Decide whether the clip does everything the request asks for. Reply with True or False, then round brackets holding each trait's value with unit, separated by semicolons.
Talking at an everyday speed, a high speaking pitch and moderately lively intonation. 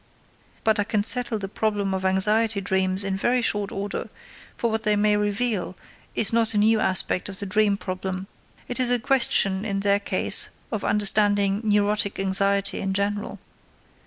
False (170 wpm; 205 Hz; 1.7 semitones)